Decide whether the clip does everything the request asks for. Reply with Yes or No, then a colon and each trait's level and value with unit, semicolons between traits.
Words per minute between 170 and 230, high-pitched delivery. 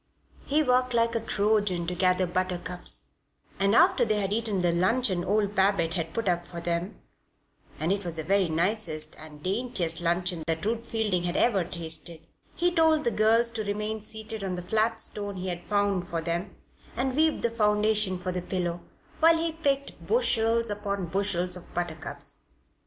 Yes: average, 180 wpm; high, 200 Hz